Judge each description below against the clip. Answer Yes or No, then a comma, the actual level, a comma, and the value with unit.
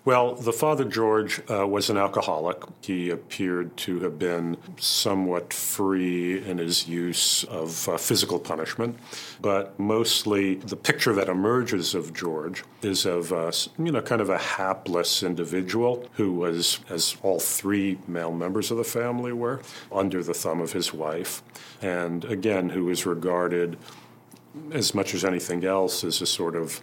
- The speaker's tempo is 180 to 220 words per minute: No, average, 160 wpm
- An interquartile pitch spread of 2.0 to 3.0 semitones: No, average, 4.1 semitones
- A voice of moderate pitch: No, very low, 95 Hz